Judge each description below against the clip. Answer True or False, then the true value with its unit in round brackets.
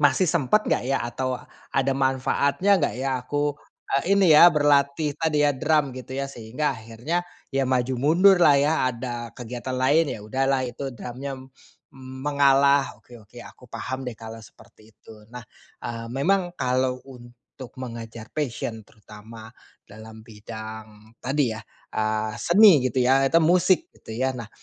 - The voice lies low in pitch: True (130 Hz)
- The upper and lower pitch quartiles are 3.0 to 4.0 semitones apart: True (3.7 semitones)